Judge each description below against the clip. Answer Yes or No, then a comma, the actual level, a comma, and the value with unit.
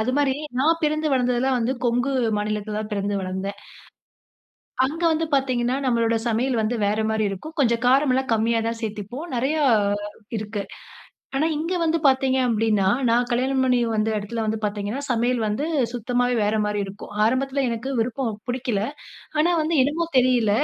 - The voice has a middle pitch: No, high, 245 Hz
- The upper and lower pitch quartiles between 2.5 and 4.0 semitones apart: Yes, average, 3.6 semitones